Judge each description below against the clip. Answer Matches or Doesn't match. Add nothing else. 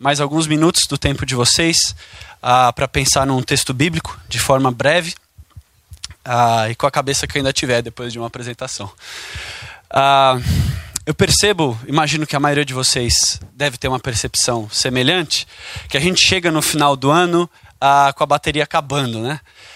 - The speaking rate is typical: Matches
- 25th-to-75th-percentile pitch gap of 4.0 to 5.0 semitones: Doesn't match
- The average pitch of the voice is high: Doesn't match